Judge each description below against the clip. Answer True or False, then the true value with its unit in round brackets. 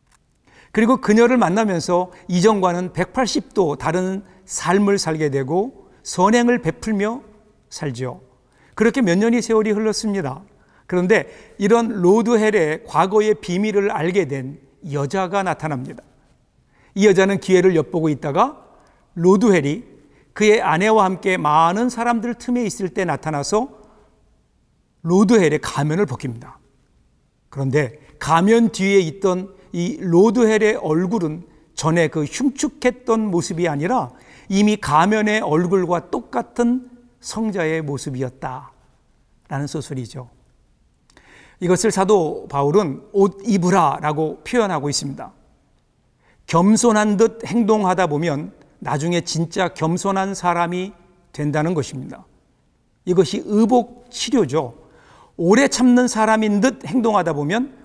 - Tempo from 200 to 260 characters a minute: True (255 characters per minute)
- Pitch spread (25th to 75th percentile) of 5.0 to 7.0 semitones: True (5.5 semitones)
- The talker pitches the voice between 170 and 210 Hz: True (190 Hz)